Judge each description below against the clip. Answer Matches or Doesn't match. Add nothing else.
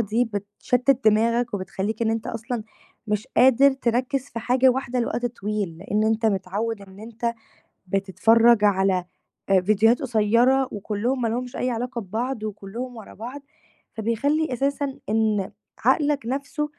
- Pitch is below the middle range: Doesn't match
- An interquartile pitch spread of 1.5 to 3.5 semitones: Matches